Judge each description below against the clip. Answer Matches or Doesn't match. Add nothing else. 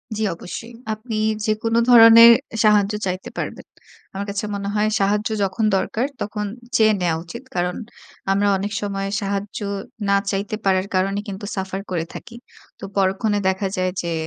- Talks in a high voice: Matches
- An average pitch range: Doesn't match